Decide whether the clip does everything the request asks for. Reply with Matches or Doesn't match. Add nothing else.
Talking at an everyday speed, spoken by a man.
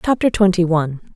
Doesn't match